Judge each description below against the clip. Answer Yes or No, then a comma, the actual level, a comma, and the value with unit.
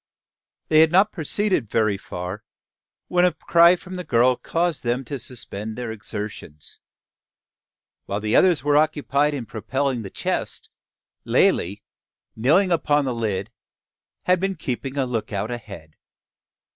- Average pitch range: No, wide, 6.8 semitones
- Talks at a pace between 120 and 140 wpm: Yes, slow, 135 wpm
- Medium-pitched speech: No, low, 130 Hz